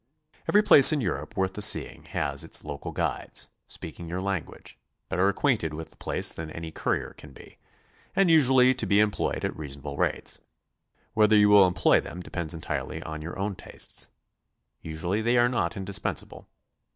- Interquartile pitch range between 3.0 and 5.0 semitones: No, wide, 5.4 semitones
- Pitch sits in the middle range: No, very low, 95 Hz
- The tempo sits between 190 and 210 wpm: No, average, 175 wpm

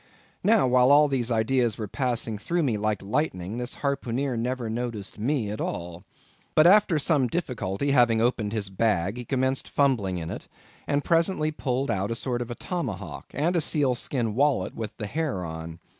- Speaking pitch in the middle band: No, low, 125 Hz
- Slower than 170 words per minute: No, average, 180 wpm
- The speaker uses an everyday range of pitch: Yes, average, 5.0 semitones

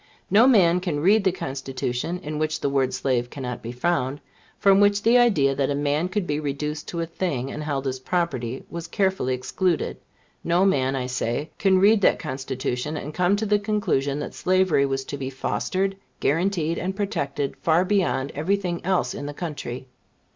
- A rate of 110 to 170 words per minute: No, average, 190 wpm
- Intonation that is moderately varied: No, wide, 5.7 semitones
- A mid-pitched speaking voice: Yes, medium, 155 Hz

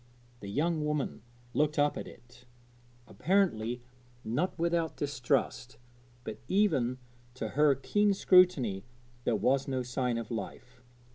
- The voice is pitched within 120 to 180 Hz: Yes, low, 135 Hz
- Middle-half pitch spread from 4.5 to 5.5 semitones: Yes, average, 4.9 semitones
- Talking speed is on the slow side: Yes, slow, 125 wpm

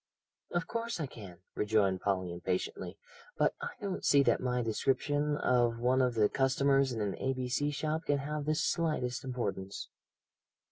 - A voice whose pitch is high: No, low, 130 Hz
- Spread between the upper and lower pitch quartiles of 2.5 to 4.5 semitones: No, average, 5.0 semitones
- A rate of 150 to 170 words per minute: Yes, average, 155 wpm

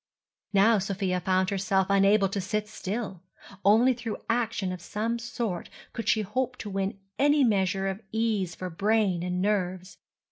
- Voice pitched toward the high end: Yes, high, 200 Hz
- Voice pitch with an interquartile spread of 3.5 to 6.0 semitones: No, average, 3.0 semitones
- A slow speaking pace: No, average, 155 wpm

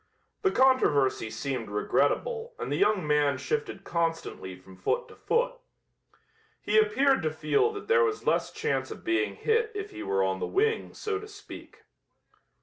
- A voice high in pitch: Yes, very high, 270 Hz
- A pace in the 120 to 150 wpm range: No, average, 165 wpm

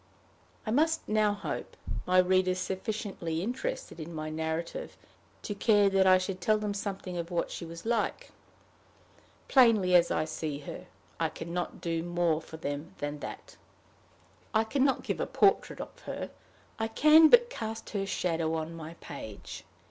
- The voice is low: No, medium, 185 Hz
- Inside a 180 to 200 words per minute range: No, average, 165 wpm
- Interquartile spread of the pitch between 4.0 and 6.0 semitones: Yes, average, 4.9 semitones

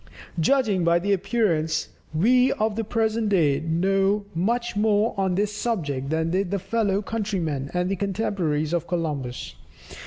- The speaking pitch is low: No, high, 195 Hz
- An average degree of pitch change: Yes, average, 4.6 semitones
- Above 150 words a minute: No, slow, 135 wpm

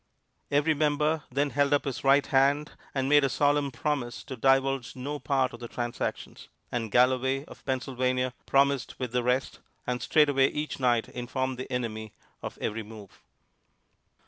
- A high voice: No, low, 135 Hz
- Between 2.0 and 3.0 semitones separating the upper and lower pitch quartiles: Yes, narrow, 2.4 semitones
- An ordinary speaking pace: Yes, average, 160 wpm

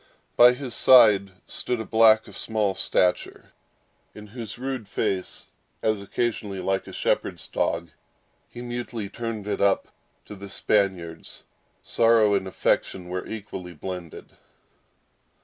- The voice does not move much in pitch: No, average, 3.2 semitones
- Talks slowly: Yes, slow, 130 wpm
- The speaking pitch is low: Yes, low, 105 Hz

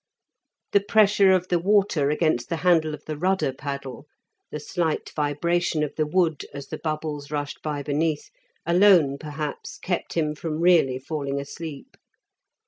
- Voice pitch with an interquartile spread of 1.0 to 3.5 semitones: Yes, average, 3.2 semitones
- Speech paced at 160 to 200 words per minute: No, average, 150 wpm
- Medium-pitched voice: Yes, medium, 155 Hz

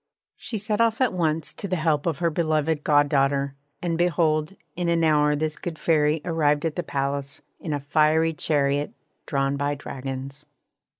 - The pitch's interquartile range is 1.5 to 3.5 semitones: Yes, narrow, 2.5 semitones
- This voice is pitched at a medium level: Yes, medium, 155 Hz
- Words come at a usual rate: Yes, average, 170 wpm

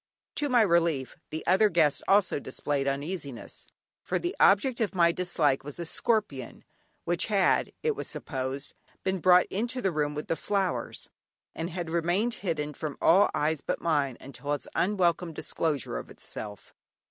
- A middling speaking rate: Yes, average, 160 wpm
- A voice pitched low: No, medium, 170 Hz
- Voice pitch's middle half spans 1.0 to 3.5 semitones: No, average, 4.9 semitones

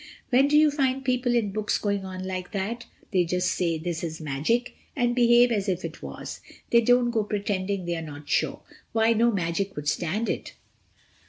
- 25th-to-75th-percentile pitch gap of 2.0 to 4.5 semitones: No, average, 5.0 semitones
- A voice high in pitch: Yes, high, 205 Hz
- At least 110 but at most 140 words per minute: No, average, 190 wpm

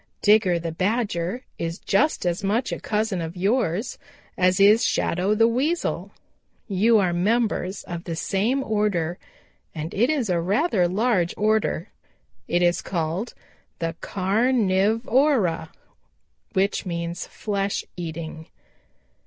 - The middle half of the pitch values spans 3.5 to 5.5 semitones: Yes, average, 4.4 semitones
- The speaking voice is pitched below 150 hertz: No, high, 195 Hz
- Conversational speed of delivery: No, slow, 130 wpm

